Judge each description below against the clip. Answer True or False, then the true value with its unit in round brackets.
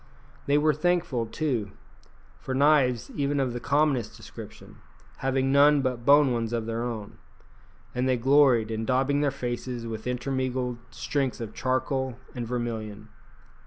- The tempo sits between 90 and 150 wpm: True (145 wpm)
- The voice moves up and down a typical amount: True (3.0 semitones)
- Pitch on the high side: False (130 Hz)